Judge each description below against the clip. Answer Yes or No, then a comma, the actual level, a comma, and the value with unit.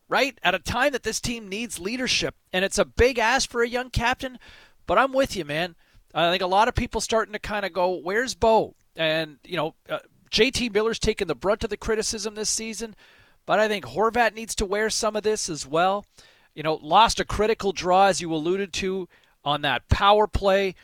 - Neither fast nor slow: No, fast, 220 wpm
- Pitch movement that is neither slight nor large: Yes, average, 3.6 semitones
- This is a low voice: No, high, 210 Hz